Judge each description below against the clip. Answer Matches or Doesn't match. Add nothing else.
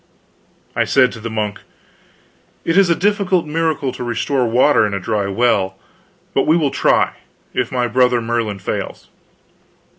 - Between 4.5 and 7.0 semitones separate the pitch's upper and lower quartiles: Matches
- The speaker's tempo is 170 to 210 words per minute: Doesn't match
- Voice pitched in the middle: Doesn't match